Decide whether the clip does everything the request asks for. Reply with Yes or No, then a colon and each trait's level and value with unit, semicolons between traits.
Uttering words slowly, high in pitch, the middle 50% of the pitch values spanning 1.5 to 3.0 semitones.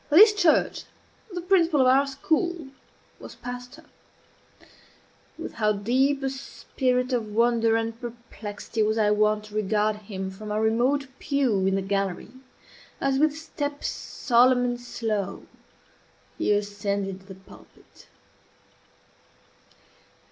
No: slow, 125 wpm; high, 235 Hz; average, 4.6 semitones